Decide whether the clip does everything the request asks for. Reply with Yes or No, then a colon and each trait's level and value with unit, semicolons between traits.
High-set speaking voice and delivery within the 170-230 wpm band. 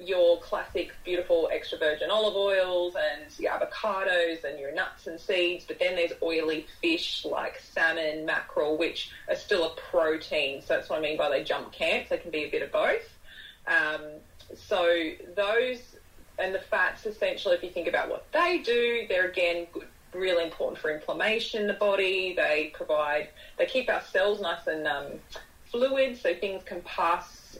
Yes: high, 200 Hz; average, 180 wpm